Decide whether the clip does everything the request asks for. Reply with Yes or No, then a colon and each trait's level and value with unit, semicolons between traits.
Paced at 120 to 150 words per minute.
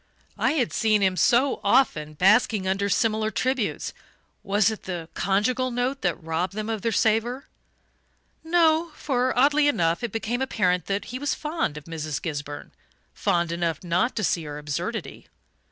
No: average, 160 wpm